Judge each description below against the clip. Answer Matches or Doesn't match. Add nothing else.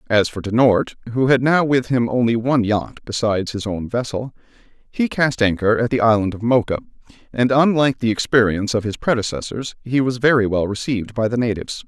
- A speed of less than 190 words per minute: Doesn't match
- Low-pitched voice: Matches